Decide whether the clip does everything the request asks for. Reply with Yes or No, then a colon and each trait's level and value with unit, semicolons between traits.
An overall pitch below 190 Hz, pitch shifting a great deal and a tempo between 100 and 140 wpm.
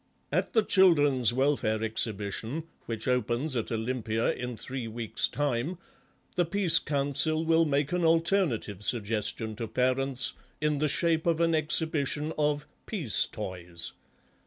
Yes: low, 135 Hz; wide, 5.8 semitones; slow, 135 wpm